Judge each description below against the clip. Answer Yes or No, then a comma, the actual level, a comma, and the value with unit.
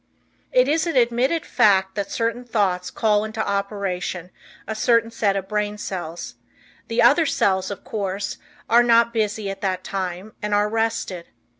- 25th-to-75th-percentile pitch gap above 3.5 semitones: No, average, 3.1 semitones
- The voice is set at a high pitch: Yes, high, 210 Hz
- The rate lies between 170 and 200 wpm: No, average, 160 wpm